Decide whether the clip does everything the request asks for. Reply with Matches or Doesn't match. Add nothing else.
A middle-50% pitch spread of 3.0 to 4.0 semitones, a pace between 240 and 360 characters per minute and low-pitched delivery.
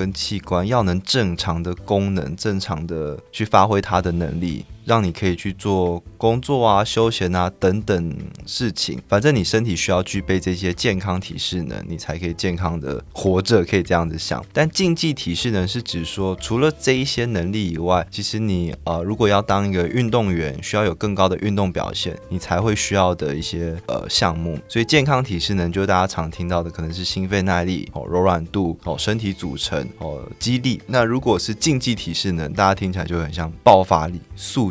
Matches